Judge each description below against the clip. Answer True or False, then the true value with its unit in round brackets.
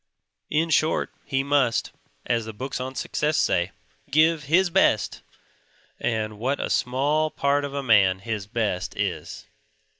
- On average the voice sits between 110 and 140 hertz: True (135 Hz)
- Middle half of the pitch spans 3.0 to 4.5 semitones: False (5.3 semitones)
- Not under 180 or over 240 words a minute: False (145 wpm)